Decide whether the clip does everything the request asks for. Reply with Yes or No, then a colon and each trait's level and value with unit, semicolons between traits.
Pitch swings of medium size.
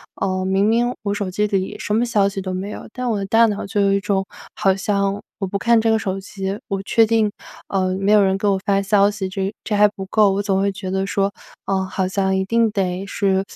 No: narrow, 1.5 semitones